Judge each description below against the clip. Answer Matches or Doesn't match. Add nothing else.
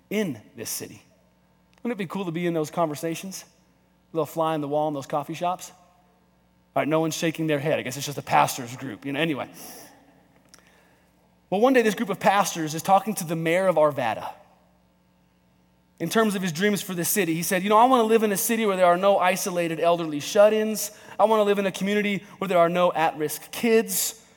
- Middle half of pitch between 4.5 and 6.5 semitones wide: Matches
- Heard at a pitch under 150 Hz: Doesn't match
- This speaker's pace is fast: Matches